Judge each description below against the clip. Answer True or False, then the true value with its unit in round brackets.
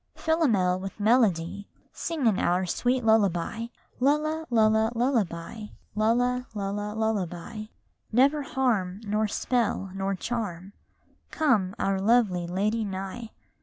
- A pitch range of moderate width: True (4.1 semitones)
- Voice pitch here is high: True (215 Hz)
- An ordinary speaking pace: False (115 wpm)